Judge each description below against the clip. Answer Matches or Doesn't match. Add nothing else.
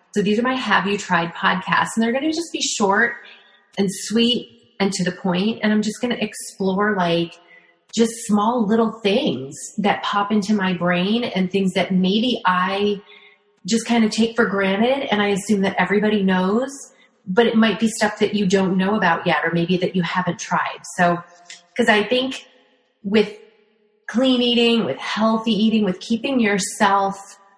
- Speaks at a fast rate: Doesn't match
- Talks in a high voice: Matches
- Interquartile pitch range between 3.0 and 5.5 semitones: Matches